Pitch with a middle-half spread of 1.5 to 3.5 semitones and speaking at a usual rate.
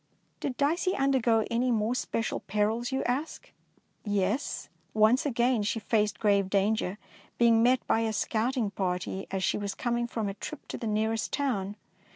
Yes: average, 3.2 semitones; average, 170 wpm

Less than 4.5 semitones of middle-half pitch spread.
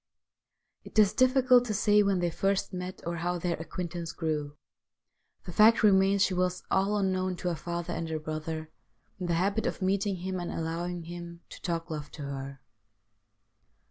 Yes: average, 3.0 semitones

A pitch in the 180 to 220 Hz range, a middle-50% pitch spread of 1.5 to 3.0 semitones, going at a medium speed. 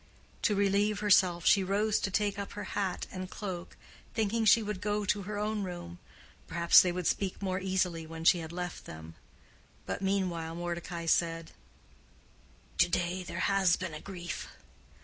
Yes: medium, 185 Hz; average, 2.7 semitones; average, 170 wpm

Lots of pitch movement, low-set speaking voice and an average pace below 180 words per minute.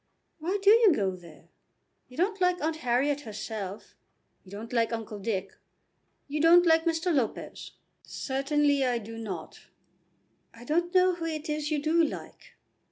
No: wide, 6.6 semitones; very high, 290 Hz; average, 160 wpm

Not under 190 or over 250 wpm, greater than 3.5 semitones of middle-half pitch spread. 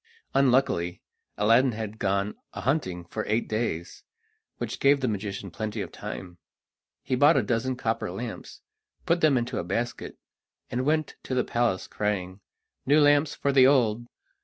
No: average, 155 wpm; average, 4.7 semitones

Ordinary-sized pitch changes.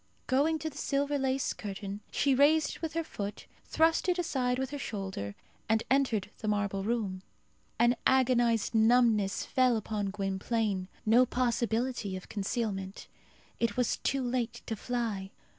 Yes: average, 4.3 semitones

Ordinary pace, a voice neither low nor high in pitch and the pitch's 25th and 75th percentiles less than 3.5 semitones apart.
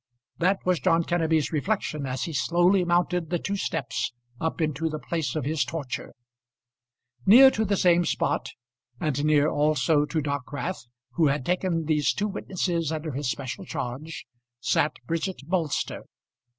Yes: average, 150 wpm; medium, 160 Hz; average, 3.1 semitones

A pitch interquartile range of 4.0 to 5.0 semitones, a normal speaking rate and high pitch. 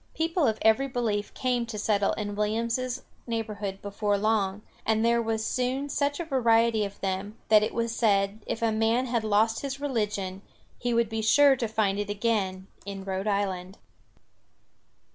No: narrow, 2.5 semitones; average, 170 wpm; high, 220 Hz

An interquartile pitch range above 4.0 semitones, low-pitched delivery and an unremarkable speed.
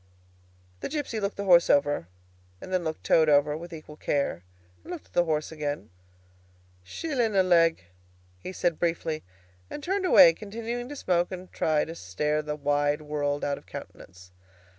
No: average, 4.6 semitones; medium, 165 Hz; average, 175 wpm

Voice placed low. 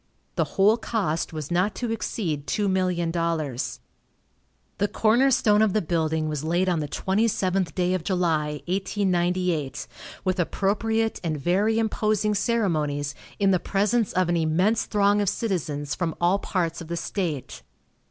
No: medium, 185 Hz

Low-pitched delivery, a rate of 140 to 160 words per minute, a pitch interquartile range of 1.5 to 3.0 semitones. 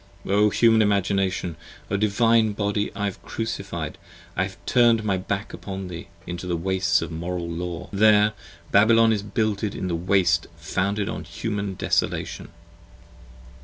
Yes: low, 100 Hz; average, 145 wpm; average, 2.7 semitones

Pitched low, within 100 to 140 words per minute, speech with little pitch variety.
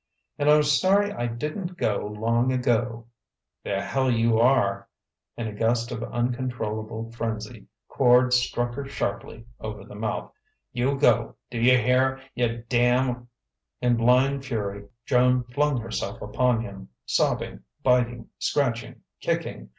Yes: low, 120 Hz; slow, 135 wpm; narrow, 2.2 semitones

